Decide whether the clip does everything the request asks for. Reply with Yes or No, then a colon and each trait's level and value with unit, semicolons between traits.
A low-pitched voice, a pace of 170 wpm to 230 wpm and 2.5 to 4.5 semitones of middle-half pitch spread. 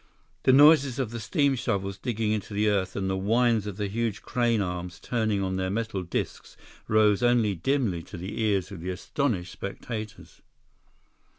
Yes: low, 105 Hz; average, 175 wpm; average, 3.6 semitones